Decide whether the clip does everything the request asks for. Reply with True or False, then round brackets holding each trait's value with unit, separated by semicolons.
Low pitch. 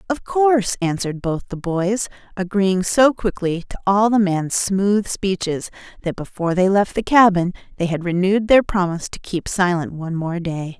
False (190 Hz)